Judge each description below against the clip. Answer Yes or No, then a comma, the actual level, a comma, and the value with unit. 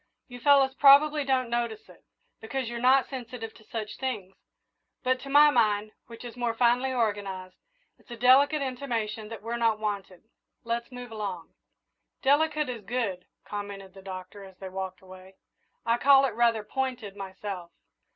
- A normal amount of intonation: Yes, average, 4.1 semitones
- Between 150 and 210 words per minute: Yes, average, 160 wpm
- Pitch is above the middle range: Yes, high, 230 Hz